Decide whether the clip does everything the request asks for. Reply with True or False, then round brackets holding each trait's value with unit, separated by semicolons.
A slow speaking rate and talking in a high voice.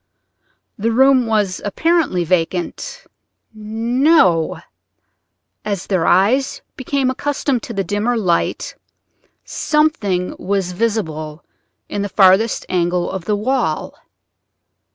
True (95 wpm; 205 Hz)